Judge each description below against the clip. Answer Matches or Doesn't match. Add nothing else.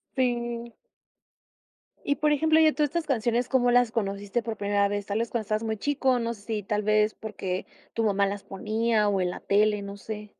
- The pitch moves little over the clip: Doesn't match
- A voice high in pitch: Matches